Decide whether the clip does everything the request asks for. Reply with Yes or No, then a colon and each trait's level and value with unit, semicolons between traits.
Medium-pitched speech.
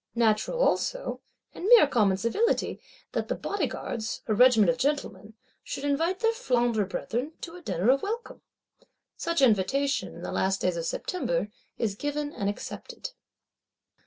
No: very high, 260 Hz